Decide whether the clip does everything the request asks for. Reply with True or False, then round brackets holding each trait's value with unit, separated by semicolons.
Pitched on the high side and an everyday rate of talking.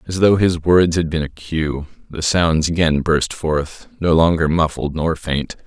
False (80 Hz; 180 wpm)